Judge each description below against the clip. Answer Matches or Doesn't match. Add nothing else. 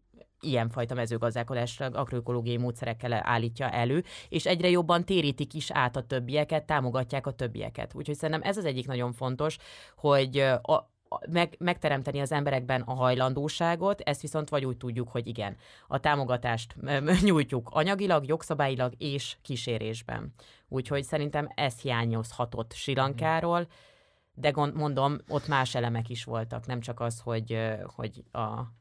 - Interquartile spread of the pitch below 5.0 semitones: Matches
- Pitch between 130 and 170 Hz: Matches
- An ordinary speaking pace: Matches